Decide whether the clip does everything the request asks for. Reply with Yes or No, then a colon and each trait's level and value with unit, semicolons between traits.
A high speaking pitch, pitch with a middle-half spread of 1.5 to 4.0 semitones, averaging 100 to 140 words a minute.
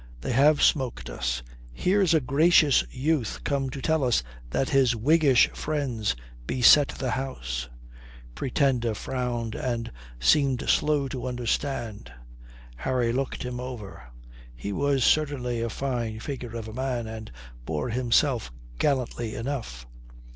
No: low, 125 Hz; average, 3.5 semitones; slow, 135 wpm